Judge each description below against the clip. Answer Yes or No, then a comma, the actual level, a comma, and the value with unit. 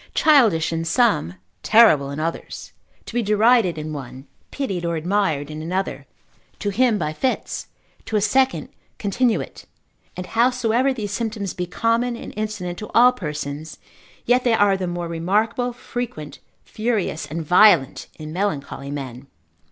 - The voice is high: Yes, high, 200 Hz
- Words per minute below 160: Yes, average, 145 wpm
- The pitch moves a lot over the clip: Yes, wide, 6.4 semitones